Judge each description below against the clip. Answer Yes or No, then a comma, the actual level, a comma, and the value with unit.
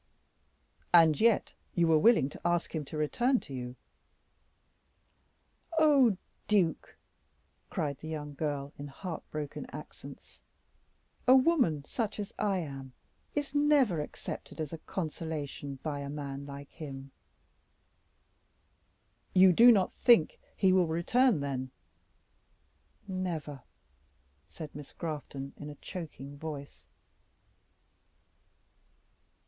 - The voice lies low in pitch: No, medium, 160 Hz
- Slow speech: Yes, slow, 110 wpm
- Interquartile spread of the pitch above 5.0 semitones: Yes, wide, 5.4 semitones